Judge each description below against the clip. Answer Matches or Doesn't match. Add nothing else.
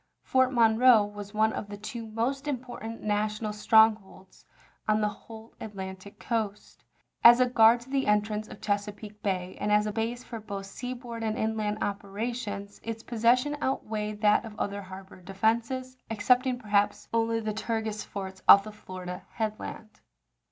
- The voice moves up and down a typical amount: Doesn't match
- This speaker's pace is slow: Doesn't match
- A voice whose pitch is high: Matches